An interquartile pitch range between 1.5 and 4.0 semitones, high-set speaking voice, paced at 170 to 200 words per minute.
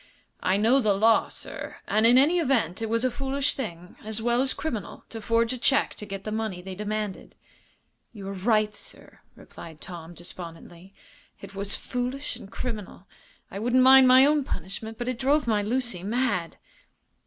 No: average, 4.5 semitones; high, 220 Hz; average, 185 wpm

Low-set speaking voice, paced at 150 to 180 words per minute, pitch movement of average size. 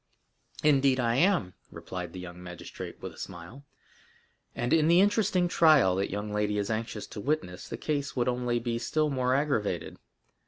No: low, 120 Hz; average, 170 wpm; wide, 6.8 semitones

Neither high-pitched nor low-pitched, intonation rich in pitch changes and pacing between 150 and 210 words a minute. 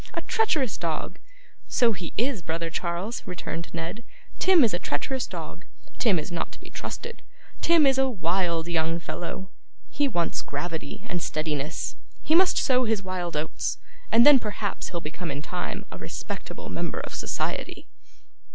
Yes: medium, 180 Hz; wide, 6.8 semitones; average, 160 wpm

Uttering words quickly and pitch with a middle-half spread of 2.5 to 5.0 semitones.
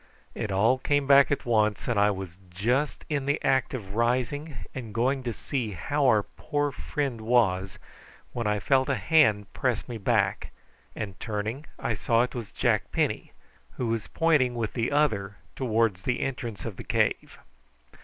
No: average, 175 wpm; average, 4.3 semitones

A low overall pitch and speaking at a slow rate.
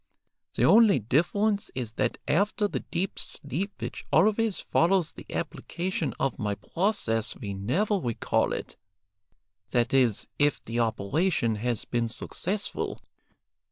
No: medium, 145 Hz; slow, 125 wpm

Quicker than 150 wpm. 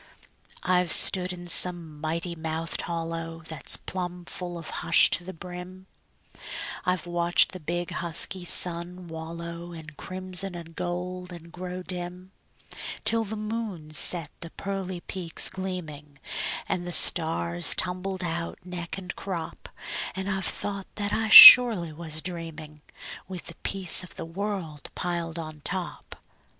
No: average, 140 wpm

